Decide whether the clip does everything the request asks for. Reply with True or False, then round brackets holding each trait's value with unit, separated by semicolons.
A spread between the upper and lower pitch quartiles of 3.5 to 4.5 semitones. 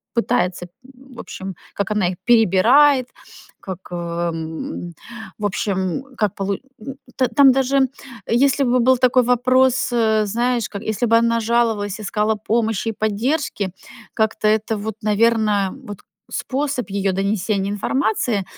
True (3.8 semitones)